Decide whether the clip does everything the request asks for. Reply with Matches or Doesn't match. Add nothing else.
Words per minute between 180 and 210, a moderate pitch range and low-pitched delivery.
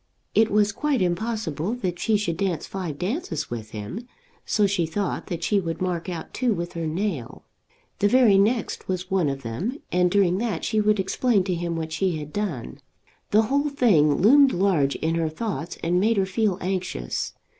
Doesn't match